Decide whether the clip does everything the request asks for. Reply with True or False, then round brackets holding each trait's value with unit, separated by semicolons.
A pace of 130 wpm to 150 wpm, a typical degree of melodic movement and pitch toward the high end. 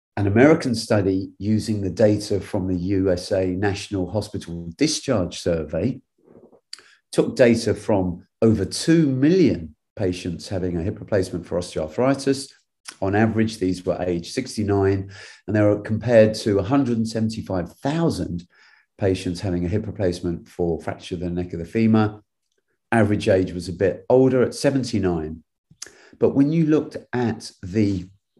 False (135 wpm; 3.6 semitones; 100 Hz)